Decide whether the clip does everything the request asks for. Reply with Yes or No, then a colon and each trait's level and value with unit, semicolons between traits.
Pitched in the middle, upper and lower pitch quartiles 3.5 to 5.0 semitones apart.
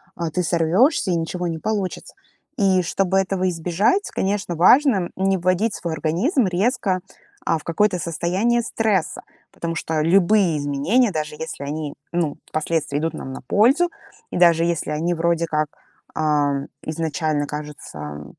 Yes: medium, 170 Hz; average, 3.8 semitones